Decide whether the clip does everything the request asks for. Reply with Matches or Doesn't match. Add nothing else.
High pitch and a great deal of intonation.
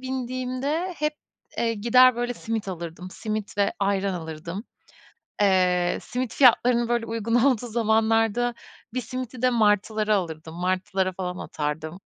Doesn't match